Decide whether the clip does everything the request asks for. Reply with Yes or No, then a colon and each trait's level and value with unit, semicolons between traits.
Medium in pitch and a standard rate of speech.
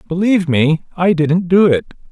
Yes: medium, 170 Hz; average, 170 wpm